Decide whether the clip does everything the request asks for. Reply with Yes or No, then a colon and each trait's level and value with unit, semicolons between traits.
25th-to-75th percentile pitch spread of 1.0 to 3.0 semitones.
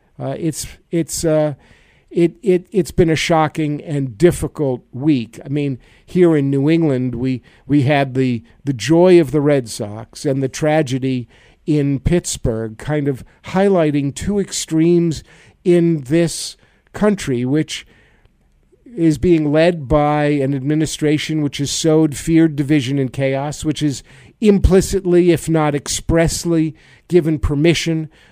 No: average, 3.4 semitones